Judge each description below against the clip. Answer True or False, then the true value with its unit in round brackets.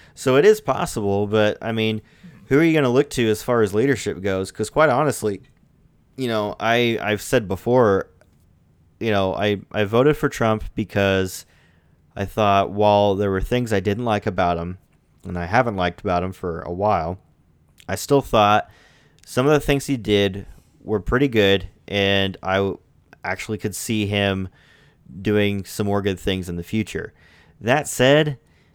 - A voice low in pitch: True (105 Hz)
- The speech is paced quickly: False (175 wpm)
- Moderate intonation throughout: True (3.4 semitones)